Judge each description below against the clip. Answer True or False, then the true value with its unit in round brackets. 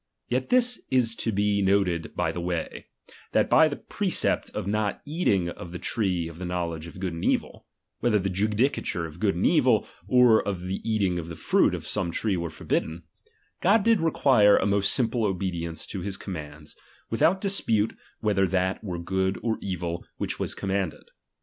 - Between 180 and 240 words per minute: True (185 wpm)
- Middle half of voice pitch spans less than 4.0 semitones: False (4.3 semitones)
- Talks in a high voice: False (95 Hz)